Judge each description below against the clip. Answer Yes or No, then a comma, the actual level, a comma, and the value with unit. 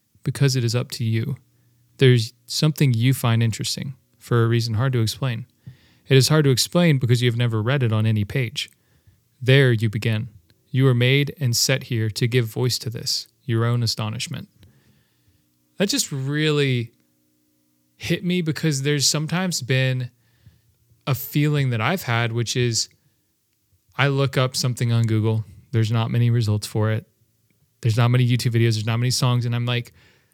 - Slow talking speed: No, average, 170 wpm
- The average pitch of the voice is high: No, low, 120 Hz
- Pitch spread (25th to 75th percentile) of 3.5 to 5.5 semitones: No, average, 2.9 semitones